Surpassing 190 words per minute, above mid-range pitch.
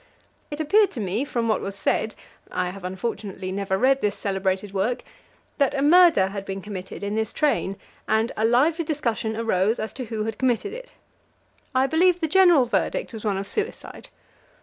No: average, 185 wpm; high, 225 Hz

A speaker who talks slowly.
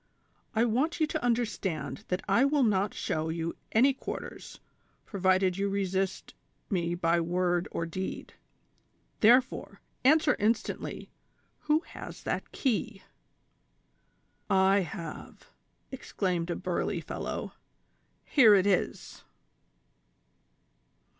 Yes: slow, 110 wpm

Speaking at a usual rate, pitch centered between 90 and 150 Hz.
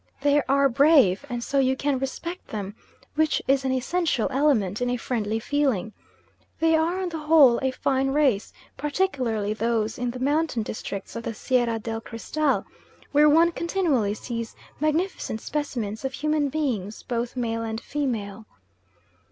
No: average, 155 wpm; very high, 260 Hz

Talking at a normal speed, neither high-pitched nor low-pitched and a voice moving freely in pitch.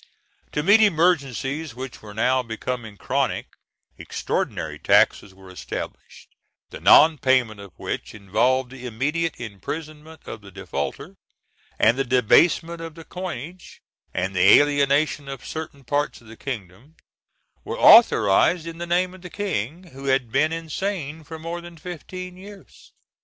Yes: average, 145 wpm; medium, 145 Hz; wide, 6.0 semitones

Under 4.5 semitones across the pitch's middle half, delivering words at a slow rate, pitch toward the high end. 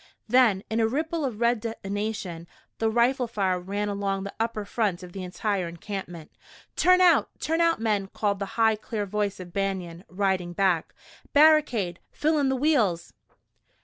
No: average, 3.9 semitones; average, 165 wpm; high, 205 Hz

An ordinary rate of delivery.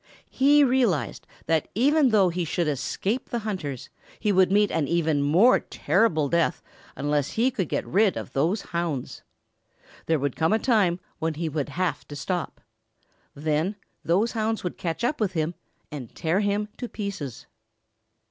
Yes: average, 165 wpm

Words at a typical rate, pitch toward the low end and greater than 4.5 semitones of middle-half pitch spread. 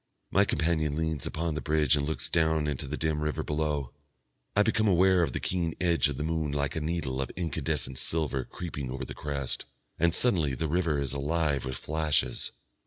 No: average, 195 wpm; very low, 75 Hz; narrow, 2.5 semitones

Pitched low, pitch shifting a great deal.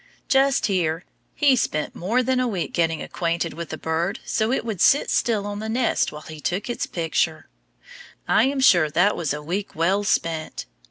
No: medium, 185 Hz; wide, 5.7 semitones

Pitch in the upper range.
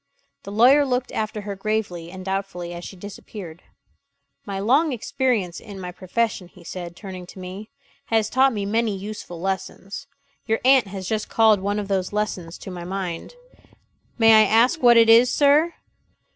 Yes: high, 205 Hz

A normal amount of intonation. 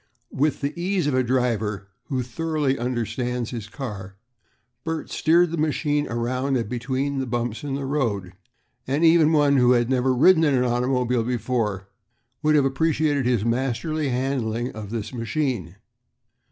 Yes: average, 3.7 semitones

